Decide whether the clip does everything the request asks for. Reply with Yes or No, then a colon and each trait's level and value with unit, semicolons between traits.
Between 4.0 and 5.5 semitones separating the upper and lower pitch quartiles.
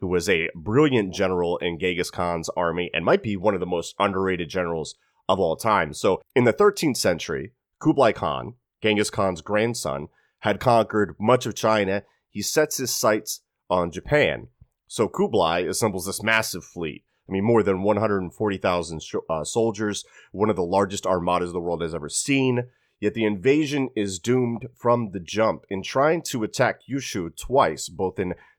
Yes: average, 4.3 semitones